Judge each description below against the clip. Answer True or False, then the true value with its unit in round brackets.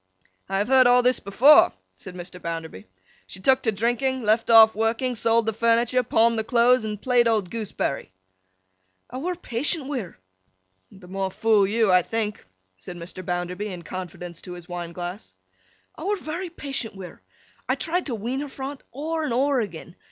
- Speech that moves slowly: False (190 wpm)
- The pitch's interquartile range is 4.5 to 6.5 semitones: True (5.6 semitones)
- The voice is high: True (225 Hz)